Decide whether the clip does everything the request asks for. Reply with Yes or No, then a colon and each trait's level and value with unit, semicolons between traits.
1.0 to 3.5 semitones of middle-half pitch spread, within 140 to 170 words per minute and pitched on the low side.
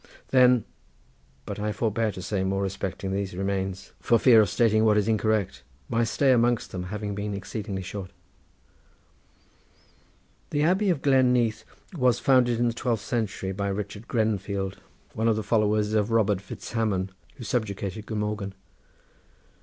Yes: average, 2.9 semitones; average, 150 wpm; low, 105 Hz